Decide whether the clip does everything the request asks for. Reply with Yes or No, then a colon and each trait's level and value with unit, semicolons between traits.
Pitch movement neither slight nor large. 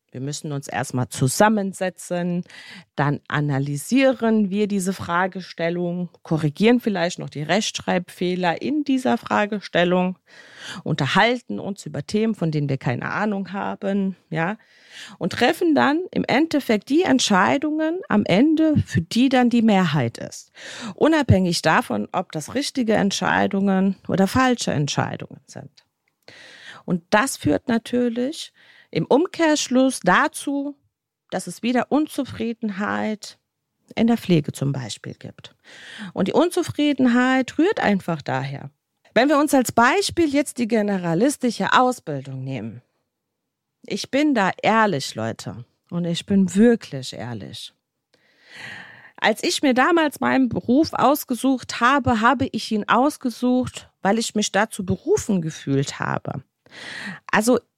No: wide, 7.3 semitones